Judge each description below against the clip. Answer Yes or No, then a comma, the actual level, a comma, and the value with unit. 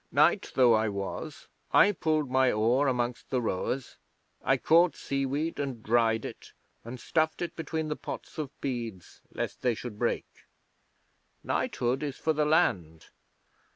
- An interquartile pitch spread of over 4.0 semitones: Yes, average, 4.8 semitones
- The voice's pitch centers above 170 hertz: No, low, 130 Hz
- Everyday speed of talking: Yes, average, 150 wpm